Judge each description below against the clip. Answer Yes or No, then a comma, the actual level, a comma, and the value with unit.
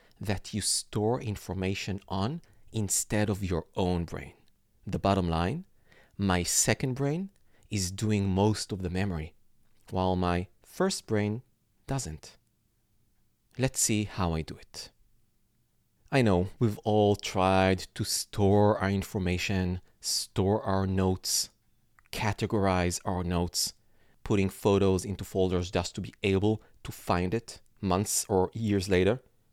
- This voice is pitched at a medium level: No, low, 100 Hz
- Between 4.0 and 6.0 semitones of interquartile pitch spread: No, average, 2.9 semitones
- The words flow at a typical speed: No, slow, 130 wpm